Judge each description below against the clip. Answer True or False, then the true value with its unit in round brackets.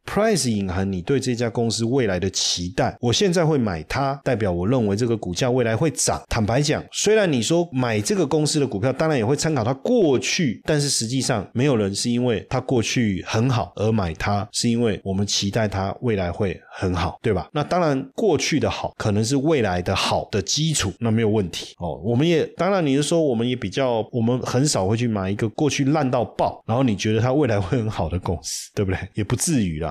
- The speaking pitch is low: True (115 Hz)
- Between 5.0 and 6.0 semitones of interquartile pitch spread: True (5.5 semitones)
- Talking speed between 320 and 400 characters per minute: True (335 characters per minute)